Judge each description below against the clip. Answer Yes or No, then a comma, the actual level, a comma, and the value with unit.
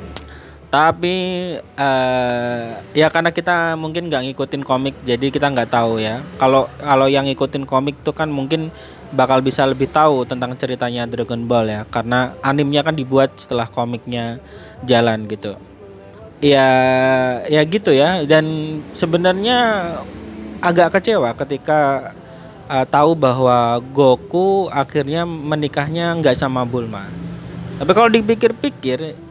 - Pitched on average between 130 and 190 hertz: Yes, low, 135 Hz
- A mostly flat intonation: No, average, 4.6 semitones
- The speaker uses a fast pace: No, average, 125 wpm